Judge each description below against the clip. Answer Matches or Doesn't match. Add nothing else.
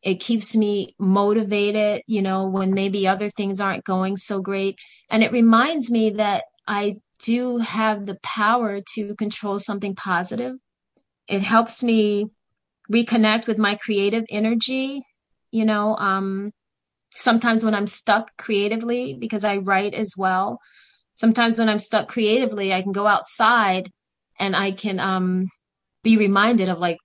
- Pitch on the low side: Doesn't match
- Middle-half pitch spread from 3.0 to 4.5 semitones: Doesn't match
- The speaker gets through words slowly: Doesn't match